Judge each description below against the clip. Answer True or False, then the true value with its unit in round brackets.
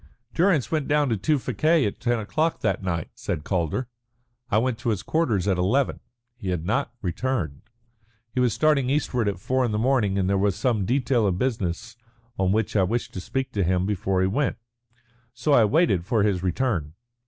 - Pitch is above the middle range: False (110 Hz)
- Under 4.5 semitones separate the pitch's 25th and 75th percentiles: False (5.6 semitones)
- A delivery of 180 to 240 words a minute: True (195 wpm)